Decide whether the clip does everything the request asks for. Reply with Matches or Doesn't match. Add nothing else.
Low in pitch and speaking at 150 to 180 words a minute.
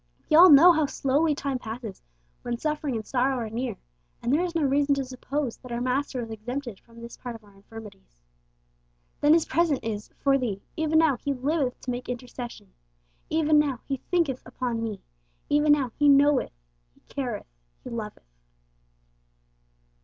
Doesn't match